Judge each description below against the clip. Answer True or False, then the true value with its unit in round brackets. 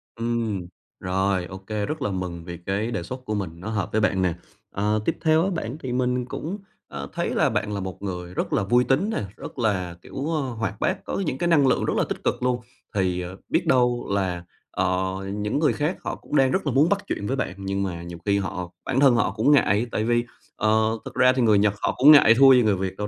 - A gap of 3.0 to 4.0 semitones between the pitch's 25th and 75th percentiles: False (5.2 semitones)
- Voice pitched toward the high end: False (110 Hz)